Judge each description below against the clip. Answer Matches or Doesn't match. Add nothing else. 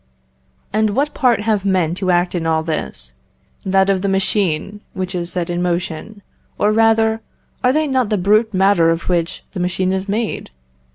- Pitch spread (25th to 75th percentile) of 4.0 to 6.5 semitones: Doesn't match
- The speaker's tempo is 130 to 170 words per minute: Doesn't match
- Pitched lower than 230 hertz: Matches